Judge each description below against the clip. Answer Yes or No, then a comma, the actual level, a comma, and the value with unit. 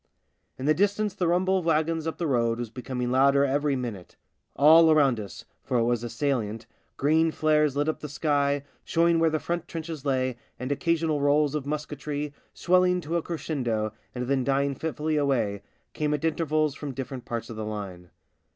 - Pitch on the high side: No, medium, 145 Hz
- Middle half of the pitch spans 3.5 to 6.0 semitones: Yes, average, 4.0 semitones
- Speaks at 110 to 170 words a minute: No, average, 195 wpm